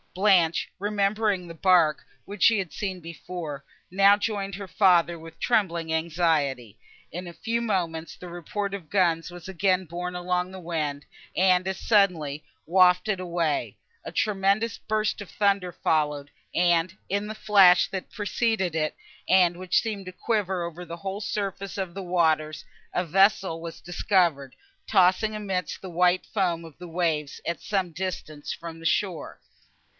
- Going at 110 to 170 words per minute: Yes, average, 160 wpm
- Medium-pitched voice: Yes, medium, 180 Hz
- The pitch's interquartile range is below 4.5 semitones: Yes, average, 3.0 semitones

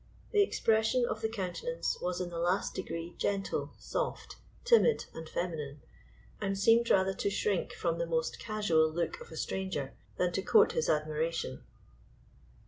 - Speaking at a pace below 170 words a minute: Yes, average, 155 wpm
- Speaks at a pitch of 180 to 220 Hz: Yes, medium, 185 Hz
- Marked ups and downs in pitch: No, average, 4.9 semitones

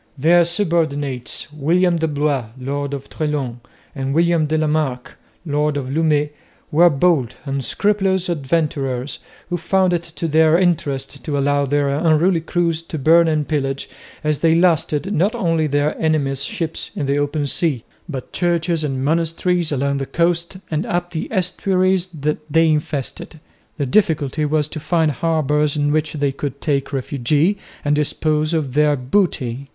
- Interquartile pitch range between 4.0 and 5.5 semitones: No, average, 3.0 semitones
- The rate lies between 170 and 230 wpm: No, average, 155 wpm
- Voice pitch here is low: No, medium, 155 Hz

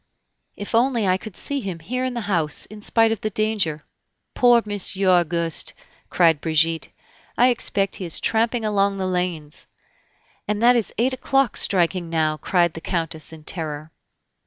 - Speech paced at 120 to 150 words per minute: No, average, 165 wpm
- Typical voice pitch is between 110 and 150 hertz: No, high, 190 Hz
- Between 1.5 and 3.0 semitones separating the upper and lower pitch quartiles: No, average, 5.3 semitones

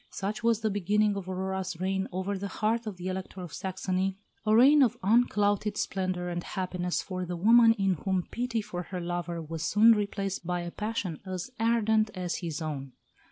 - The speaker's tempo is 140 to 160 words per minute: No, average, 190 wpm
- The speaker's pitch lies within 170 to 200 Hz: Yes, high, 190 Hz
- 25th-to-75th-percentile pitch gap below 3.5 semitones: Yes, average, 3.0 semitones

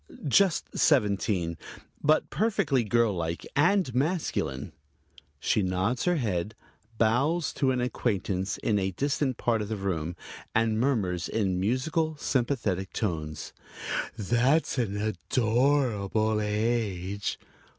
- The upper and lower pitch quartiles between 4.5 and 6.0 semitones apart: Yes, wide, 5.5 semitones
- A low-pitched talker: Yes, low, 110 Hz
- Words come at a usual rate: No, slow, 110 wpm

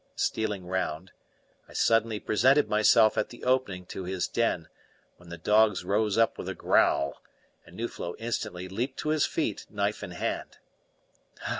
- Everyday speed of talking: Yes, average, 155 wpm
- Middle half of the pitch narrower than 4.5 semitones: Yes, average, 3.8 semitones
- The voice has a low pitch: Yes, low, 105 Hz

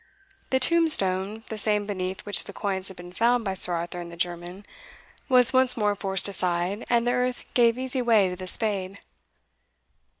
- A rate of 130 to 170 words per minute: No, average, 180 wpm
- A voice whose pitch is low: No, high, 205 Hz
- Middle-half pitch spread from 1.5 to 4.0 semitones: No, average, 4.5 semitones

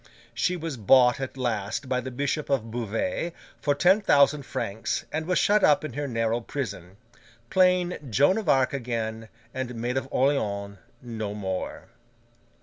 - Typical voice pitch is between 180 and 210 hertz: No, low, 130 Hz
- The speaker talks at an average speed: Yes, average, 155 wpm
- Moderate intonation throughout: Yes, average, 4.6 semitones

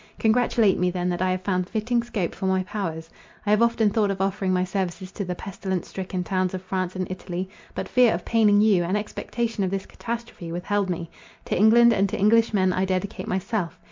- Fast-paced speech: Yes, fast, 210 wpm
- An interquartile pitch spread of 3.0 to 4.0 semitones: No, narrow, 2.6 semitones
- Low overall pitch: No, high, 190 Hz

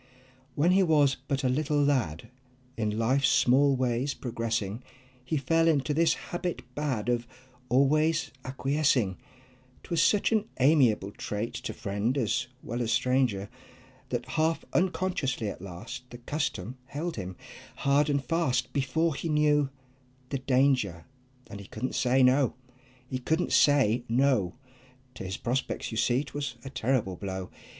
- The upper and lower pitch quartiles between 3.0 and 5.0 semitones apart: Yes, average, 4.1 semitones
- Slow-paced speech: No, average, 145 wpm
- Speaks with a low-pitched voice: Yes, low, 130 Hz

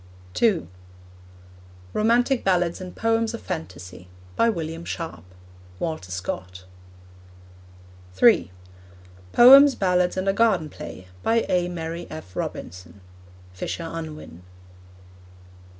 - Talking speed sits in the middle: No, slow, 100 wpm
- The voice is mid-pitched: Yes, medium, 170 Hz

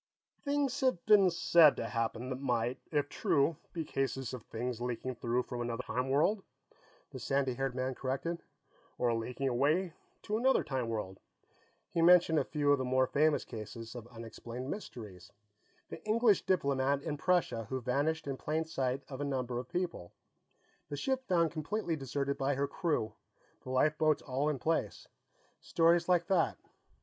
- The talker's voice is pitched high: No, medium, 140 Hz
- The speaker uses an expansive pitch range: No, average, 4.7 semitones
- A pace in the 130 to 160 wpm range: No, average, 170 wpm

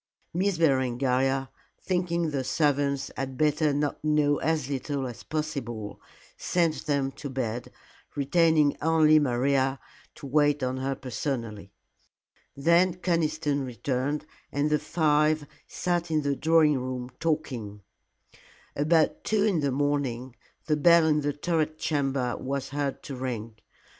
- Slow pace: Yes, slow, 130 wpm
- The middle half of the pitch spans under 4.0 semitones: Yes, average, 3.0 semitones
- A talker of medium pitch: Yes, medium, 145 Hz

